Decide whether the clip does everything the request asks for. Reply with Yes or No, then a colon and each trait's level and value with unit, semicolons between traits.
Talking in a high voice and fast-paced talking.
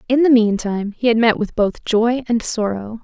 Yes: high, 225 Hz; fast, 220 wpm